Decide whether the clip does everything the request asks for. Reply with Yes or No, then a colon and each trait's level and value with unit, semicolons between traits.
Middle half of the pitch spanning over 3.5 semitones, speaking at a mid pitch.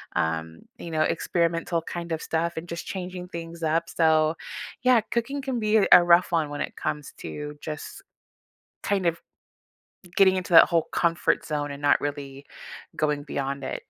No: average, 3.2 semitones; medium, 165 Hz